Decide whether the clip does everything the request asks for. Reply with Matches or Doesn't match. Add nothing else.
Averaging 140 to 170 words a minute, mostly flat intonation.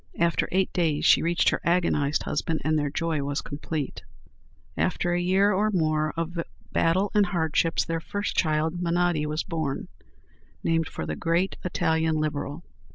Matches